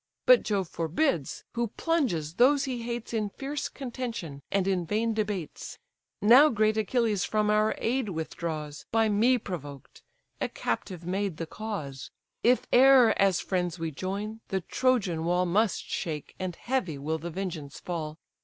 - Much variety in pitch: Yes, wide, 5.8 semitones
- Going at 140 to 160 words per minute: Yes, average, 155 wpm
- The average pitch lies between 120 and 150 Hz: No, high, 200 Hz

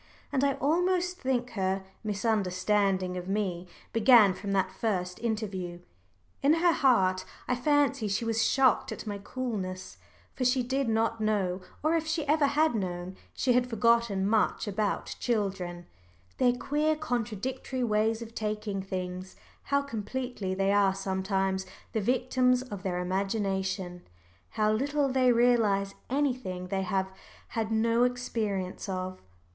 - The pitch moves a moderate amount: Yes, average, 4.8 semitones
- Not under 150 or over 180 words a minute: No, average, 140 wpm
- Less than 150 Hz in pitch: No, high, 215 Hz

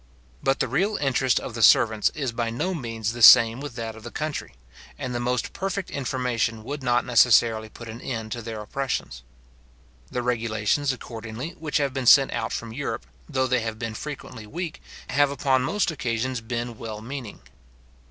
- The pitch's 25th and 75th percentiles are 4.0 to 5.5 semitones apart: No, average, 3.3 semitones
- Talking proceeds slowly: No, average, 180 wpm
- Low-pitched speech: Yes, low, 120 Hz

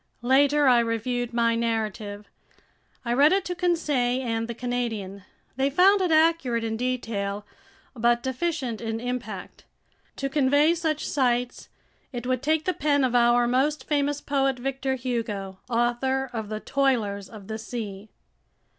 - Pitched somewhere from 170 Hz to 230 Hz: No, high, 245 Hz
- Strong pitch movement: No, average, 3.6 semitones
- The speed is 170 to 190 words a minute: No, average, 145 wpm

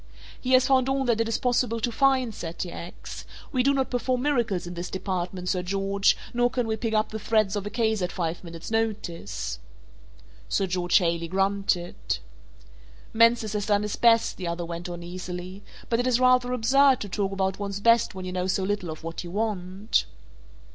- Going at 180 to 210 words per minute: Yes, average, 200 wpm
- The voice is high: Yes, high, 200 Hz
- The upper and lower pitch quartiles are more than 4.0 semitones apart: Yes, average, 4.5 semitones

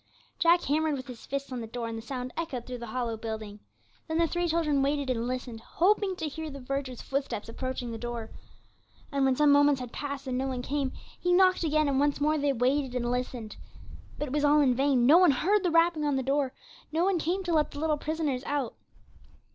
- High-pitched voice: Yes, very high, 275 Hz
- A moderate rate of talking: No, fast, 230 wpm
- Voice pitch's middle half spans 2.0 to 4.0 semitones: Yes, average, 3.7 semitones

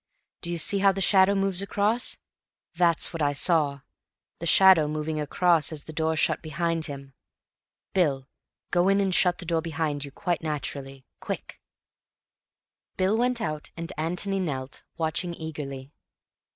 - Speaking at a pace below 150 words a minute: Yes, average, 140 wpm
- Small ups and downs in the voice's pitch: No, average, 3.8 semitones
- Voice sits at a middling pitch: Yes, medium, 165 Hz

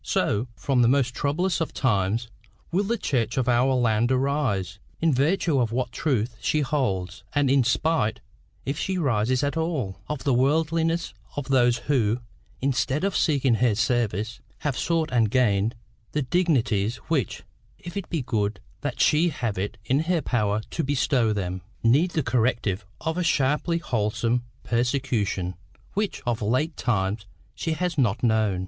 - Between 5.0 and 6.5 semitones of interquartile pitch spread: Yes, average, 5.3 semitones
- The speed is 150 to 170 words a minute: Yes, average, 160 wpm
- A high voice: No, low, 130 Hz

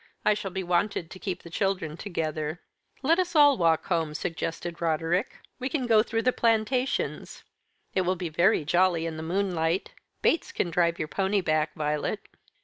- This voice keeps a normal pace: Yes, average, 175 wpm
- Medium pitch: Yes, medium, 180 Hz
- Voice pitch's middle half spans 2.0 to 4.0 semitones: No, average, 4.4 semitones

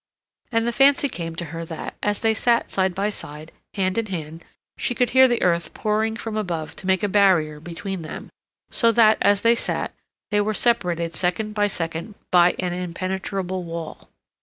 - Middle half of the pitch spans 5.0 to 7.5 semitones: No, average, 4.4 semitones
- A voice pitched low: No, high, 190 Hz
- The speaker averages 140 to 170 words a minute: No, average, 185 wpm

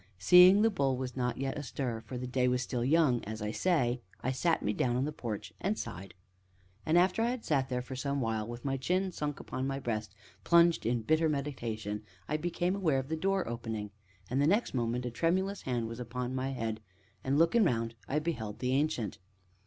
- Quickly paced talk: Yes, fast, 215 wpm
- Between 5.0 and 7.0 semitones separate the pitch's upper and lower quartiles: Yes, average, 5.3 semitones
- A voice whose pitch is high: No, low, 130 Hz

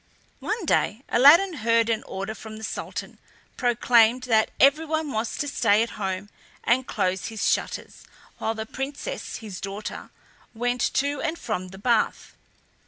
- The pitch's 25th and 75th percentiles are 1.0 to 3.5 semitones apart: No, average, 4.3 semitones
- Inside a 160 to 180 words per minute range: No, average, 150 wpm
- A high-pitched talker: Yes, high, 230 Hz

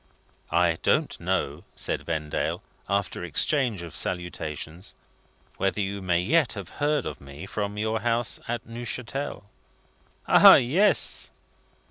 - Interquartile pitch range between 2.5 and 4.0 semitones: No, wide, 5.5 semitones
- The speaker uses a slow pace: Yes, slow, 120 wpm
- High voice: No, low, 100 Hz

